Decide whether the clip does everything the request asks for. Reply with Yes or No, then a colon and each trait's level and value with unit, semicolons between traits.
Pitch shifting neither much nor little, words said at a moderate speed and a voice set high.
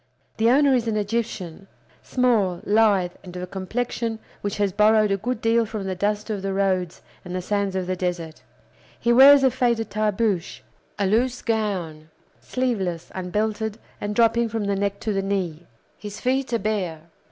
Yes: average, 3.4 semitones; average, 175 wpm; high, 205 Hz